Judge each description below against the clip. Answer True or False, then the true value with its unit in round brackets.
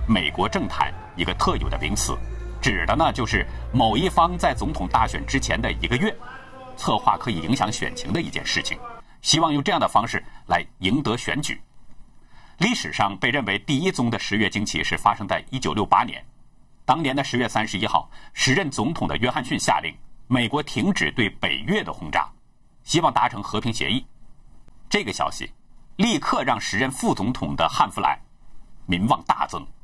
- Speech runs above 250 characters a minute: True (275 characters per minute)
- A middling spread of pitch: False (7.8 semitones)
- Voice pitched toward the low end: True (125 Hz)